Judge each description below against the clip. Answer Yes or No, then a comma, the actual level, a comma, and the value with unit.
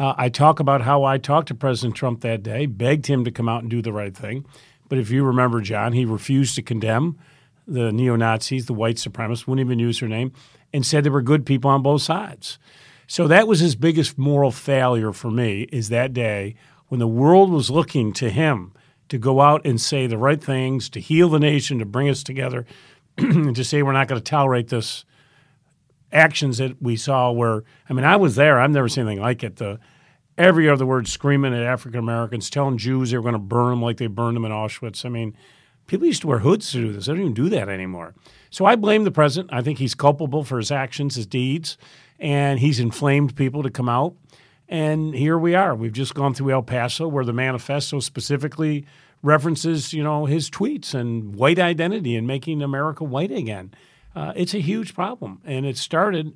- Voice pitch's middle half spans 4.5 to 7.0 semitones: No, average, 3.7 semitones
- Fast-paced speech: Yes, fast, 220 wpm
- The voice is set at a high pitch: No, low, 135 Hz